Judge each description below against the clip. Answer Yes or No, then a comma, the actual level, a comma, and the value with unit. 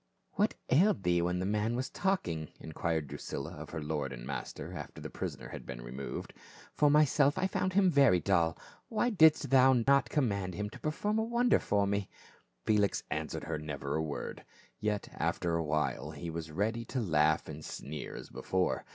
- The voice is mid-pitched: No, low, 100 Hz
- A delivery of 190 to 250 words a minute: Yes, average, 195 wpm